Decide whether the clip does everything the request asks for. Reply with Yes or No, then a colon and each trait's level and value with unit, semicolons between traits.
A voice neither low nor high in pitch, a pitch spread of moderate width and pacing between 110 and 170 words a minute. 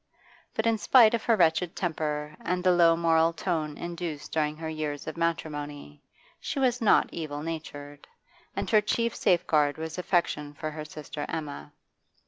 Yes: medium, 160 Hz; average, 3.0 semitones; average, 160 wpm